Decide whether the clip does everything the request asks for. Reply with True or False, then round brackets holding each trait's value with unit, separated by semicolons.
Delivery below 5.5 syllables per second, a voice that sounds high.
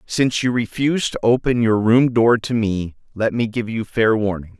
False (5.0 syllables/s; 115 Hz)